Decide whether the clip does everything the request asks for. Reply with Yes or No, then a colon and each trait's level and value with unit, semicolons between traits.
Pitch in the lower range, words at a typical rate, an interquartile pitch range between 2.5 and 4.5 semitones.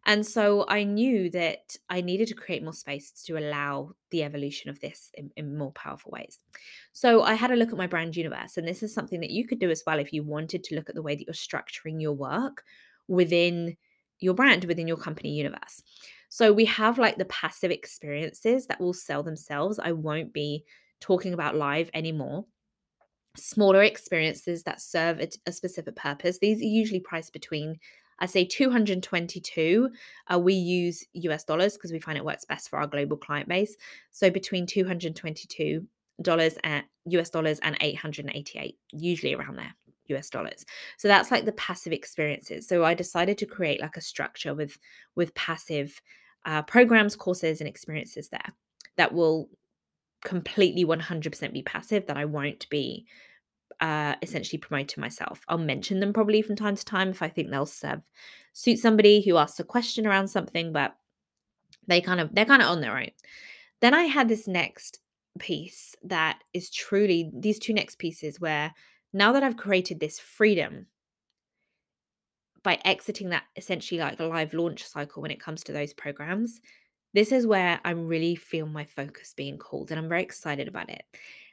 No: medium, 175 Hz; average, 180 wpm; average, 4.2 semitones